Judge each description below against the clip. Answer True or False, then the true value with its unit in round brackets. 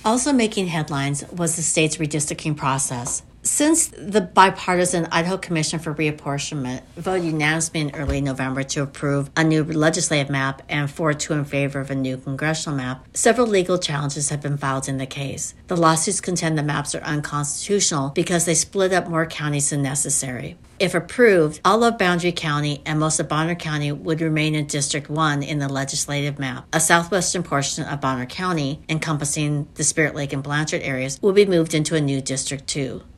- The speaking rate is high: False (185 wpm)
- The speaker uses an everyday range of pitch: True (3.2 semitones)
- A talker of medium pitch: True (155 Hz)